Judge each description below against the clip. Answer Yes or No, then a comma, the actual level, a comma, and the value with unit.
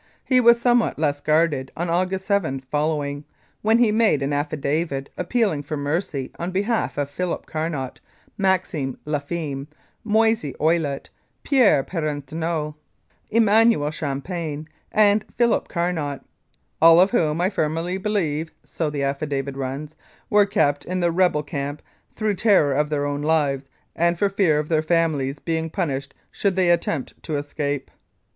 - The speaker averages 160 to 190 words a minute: No, average, 145 wpm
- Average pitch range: Yes, average, 4.5 semitones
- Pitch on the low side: No, medium, 160 Hz